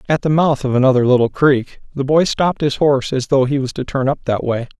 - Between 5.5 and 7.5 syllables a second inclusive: Yes, 6.0 syllables/s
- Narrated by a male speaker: Yes, male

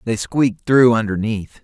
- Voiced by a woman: No, male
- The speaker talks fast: No, average, 145 wpm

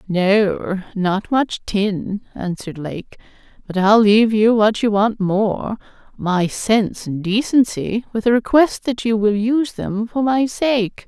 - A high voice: Yes, high, 215 Hz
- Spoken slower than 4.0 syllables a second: Yes, 3.8 syllables/s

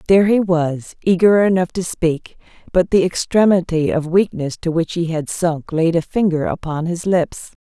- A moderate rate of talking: Yes, average, 180 wpm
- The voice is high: No, medium, 170 Hz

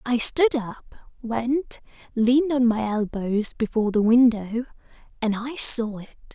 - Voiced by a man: No, female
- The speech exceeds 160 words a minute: No, average, 140 wpm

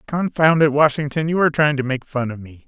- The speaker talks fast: Yes, fast, 245 wpm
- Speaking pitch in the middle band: Yes, medium, 145 Hz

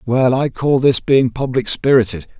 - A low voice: Yes, low, 125 Hz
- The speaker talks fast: No, average, 175 wpm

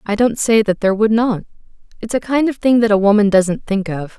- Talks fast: Yes, fast, 260 wpm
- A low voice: No, high, 215 Hz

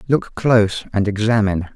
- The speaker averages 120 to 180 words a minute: Yes, slow, 135 wpm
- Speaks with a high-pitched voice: No, low, 105 Hz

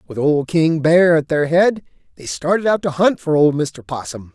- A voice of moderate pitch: Yes, medium, 155 Hz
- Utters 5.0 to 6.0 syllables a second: No, 4.7 syllables/s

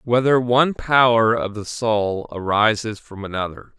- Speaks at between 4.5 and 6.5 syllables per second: No, 4.3 syllables/s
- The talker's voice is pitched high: No, low, 110 Hz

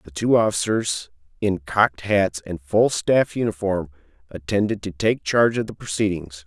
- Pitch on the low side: Yes, very low, 95 Hz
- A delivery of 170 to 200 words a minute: No, average, 160 wpm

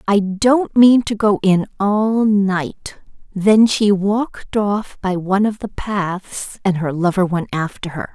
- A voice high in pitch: Yes, high, 200 Hz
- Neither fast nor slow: Yes, average, 170 wpm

